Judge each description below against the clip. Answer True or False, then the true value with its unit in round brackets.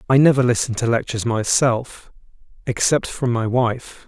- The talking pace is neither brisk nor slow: False (130 wpm)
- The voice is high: False (120 Hz)